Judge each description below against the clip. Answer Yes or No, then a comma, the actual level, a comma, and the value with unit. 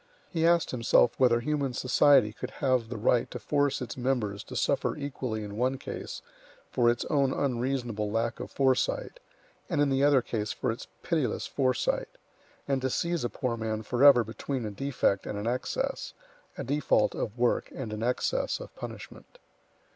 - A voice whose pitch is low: Yes, low, 125 Hz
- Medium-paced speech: Yes, average, 175 wpm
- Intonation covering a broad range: No, average, 3.4 semitones